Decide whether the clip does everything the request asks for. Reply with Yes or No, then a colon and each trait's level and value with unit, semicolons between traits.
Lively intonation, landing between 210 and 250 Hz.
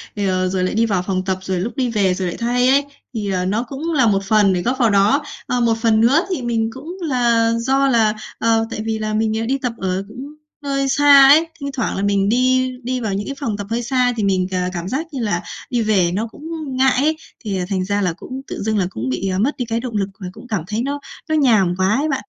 No: average, 4.8 semitones; high, 225 Hz